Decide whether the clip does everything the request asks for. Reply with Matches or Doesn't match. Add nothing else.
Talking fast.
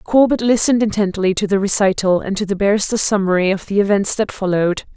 Doesn't match